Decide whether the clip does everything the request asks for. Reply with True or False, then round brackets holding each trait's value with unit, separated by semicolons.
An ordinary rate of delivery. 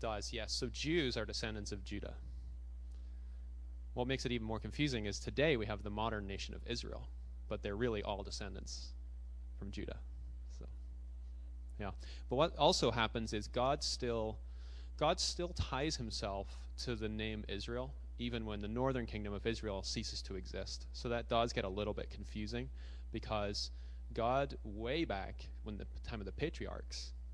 True (165 wpm)